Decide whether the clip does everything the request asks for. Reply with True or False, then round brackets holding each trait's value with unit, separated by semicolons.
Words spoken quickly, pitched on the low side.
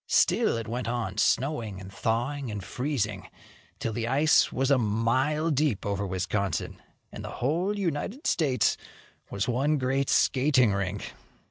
False (145 wpm; 125 Hz)